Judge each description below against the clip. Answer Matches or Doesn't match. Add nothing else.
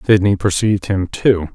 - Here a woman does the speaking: Doesn't match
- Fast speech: Doesn't match